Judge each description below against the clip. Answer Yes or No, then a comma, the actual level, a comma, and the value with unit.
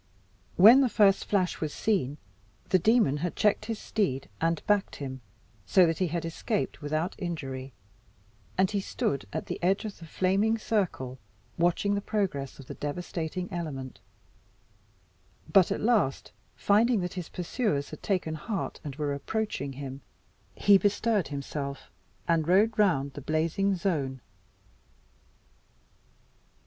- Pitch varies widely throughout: Yes, wide, 5.9 semitones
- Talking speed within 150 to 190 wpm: No, average, 140 wpm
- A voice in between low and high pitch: Yes, medium, 175 Hz